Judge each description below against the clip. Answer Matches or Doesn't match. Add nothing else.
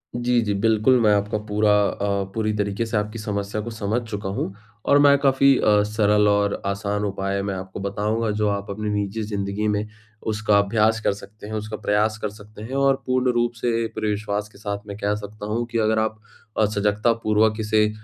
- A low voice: Matches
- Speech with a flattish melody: Matches